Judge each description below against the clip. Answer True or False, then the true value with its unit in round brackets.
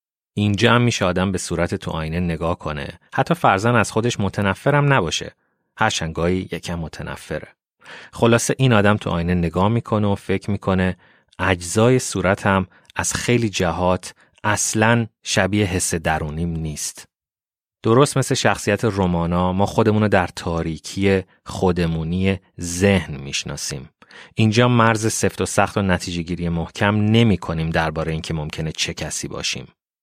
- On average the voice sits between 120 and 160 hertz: False (95 Hz)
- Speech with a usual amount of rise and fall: True (4.3 semitones)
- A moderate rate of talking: True (135 wpm)